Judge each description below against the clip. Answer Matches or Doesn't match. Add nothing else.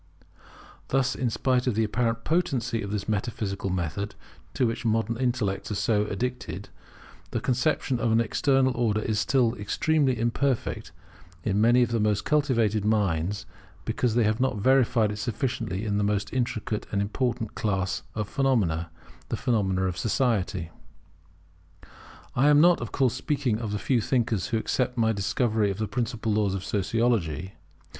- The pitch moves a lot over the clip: Doesn't match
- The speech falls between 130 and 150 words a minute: Doesn't match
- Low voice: Matches